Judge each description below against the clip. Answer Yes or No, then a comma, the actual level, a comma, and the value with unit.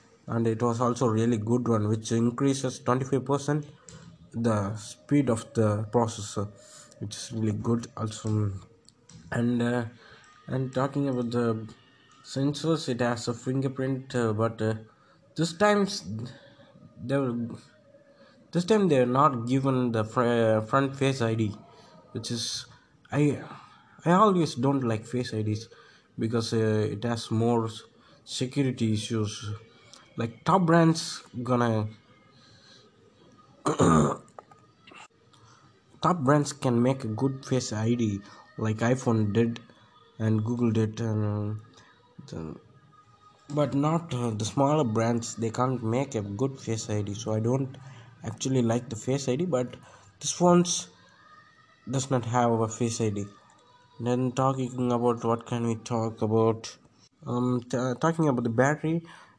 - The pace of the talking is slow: Yes, slow, 130 wpm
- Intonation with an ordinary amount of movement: Yes, average, 3.3 semitones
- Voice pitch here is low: Yes, low, 120 Hz